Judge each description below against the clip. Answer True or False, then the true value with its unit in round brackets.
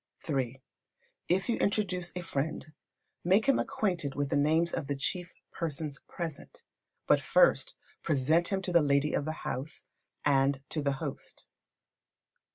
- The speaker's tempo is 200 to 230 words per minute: False (150 wpm)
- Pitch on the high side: False (155 Hz)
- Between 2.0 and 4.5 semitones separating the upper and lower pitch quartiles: True (3.9 semitones)